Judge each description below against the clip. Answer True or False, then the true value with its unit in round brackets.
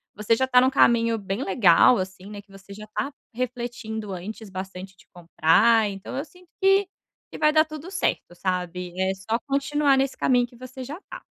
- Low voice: False (225 Hz)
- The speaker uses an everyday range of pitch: False (5.8 semitones)